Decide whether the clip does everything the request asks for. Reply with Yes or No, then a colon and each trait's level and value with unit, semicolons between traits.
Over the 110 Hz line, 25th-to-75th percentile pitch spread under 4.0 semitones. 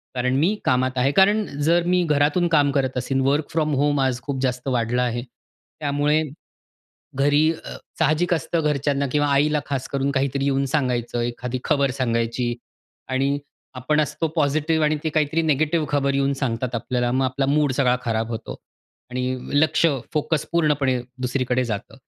Yes: medium, 140 Hz; average, 3.0 semitones